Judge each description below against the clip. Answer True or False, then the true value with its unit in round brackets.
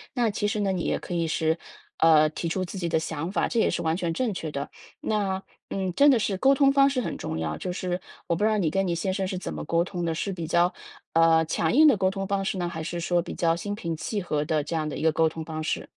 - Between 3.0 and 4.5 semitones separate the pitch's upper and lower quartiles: True (3.3 semitones)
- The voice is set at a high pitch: False (175 Hz)